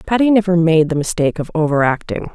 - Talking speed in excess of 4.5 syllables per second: Yes, 6.4 syllables/s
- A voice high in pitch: No, medium, 170 Hz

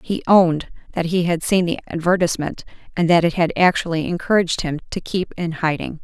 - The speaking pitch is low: No, medium, 170 Hz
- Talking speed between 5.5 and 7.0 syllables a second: Yes, 5.9 syllables/s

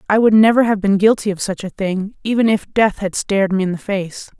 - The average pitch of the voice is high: Yes, high, 200 Hz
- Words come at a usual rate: No, fast, 260 wpm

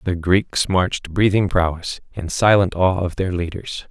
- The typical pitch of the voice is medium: No, very low, 90 Hz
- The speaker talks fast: No, average, 170 wpm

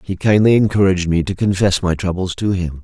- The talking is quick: Yes, fast, 210 wpm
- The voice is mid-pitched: No, very low, 95 Hz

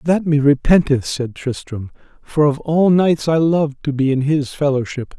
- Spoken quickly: No, average, 185 wpm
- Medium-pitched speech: Yes, medium, 145 Hz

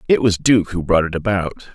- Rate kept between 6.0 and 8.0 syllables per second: No, 5.8 syllables/s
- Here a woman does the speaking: No, male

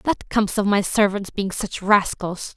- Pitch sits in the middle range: No, high, 200 Hz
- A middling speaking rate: Yes, average, 190 wpm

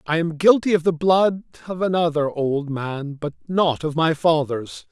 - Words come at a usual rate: Yes, average, 185 wpm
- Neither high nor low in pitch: Yes, medium, 160 Hz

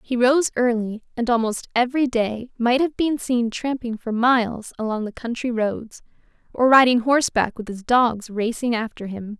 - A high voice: Yes, high, 235 Hz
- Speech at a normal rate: Yes, average, 175 wpm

